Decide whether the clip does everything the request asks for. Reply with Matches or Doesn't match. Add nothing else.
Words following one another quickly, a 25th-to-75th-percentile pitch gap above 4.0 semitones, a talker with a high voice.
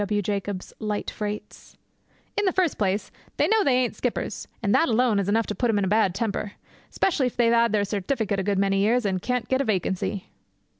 Doesn't match